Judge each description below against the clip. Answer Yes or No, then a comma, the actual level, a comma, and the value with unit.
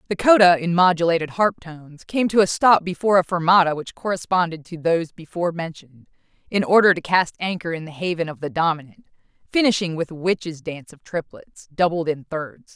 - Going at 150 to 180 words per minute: No, average, 190 wpm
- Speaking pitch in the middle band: Yes, medium, 170 Hz